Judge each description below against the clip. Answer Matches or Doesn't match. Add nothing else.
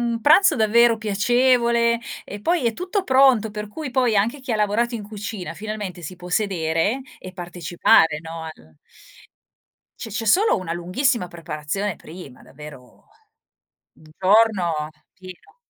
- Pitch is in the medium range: Doesn't match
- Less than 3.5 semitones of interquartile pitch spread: Doesn't match